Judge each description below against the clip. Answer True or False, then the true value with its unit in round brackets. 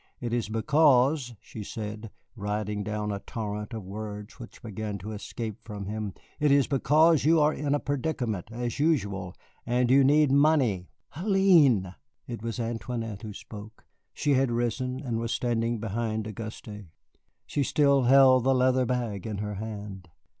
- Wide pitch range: False (4.2 semitones)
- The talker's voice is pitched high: False (115 Hz)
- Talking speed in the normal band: True (160 wpm)